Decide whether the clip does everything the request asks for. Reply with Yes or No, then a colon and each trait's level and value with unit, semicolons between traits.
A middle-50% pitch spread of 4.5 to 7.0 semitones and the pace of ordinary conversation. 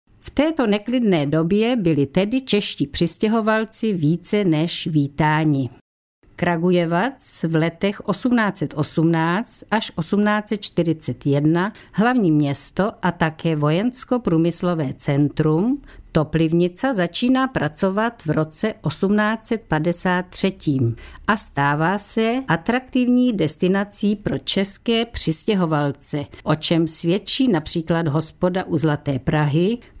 No: wide, 5.5 semitones; slow, 90 wpm